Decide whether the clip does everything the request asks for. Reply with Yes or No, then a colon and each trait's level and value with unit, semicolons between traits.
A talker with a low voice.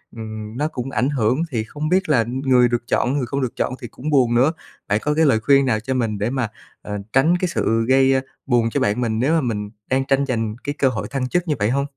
Yes: low, 130 Hz